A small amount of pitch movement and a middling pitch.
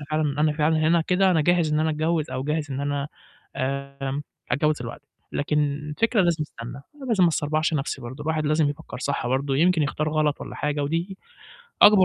Yes: narrow, 2.3 semitones; medium, 150 Hz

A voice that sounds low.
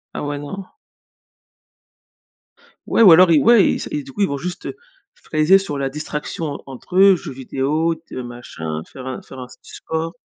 No: medium, 155 Hz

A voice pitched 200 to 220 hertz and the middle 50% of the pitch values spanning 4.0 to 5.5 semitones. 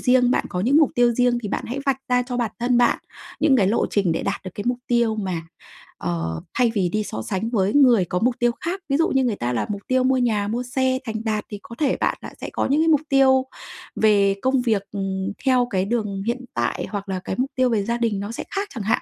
No: high, 235 Hz; average, 4.3 semitones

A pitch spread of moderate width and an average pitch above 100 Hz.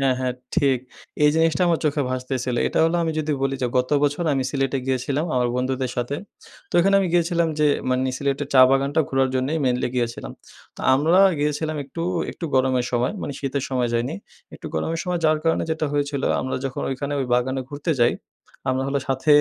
Yes: average, 3.0 semitones; low, 135 Hz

